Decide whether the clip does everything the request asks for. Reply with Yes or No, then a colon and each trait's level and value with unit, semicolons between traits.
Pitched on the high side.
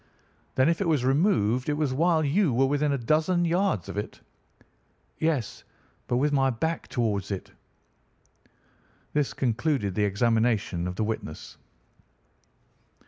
No: low, 135 Hz